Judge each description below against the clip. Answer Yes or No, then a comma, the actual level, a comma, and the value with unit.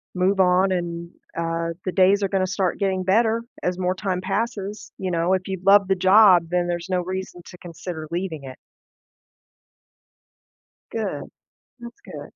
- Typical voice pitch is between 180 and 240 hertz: Yes, medium, 185 Hz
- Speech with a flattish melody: Yes, narrow, 1.8 semitones